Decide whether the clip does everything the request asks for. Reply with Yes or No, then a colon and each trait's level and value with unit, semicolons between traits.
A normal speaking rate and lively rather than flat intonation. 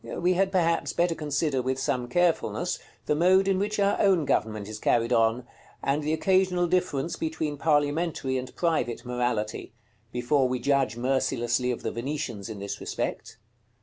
Yes: average, 160 wpm; wide, 5.7 semitones